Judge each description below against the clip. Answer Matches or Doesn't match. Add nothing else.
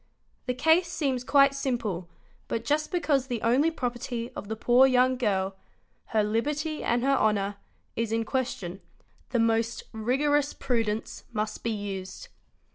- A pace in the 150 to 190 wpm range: Doesn't match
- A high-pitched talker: Matches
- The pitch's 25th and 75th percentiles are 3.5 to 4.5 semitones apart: Matches